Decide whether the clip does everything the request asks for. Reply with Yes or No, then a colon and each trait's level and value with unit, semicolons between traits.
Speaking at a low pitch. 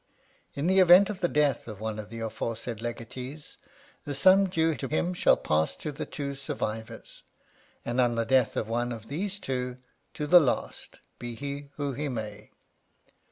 Yes: low, 130 Hz